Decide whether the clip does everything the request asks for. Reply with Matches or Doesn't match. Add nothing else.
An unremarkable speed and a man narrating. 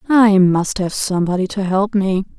Doesn't match